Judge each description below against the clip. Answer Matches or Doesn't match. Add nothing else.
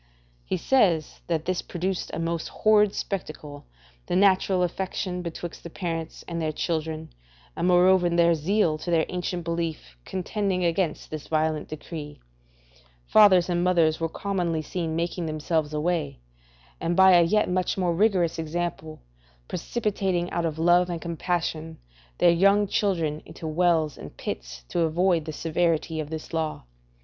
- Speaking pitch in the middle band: Matches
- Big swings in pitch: Doesn't match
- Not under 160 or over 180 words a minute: Doesn't match